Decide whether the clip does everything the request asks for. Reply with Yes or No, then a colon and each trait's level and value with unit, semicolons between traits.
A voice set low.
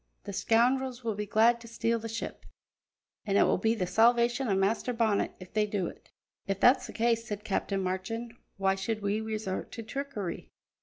No: high, 220 Hz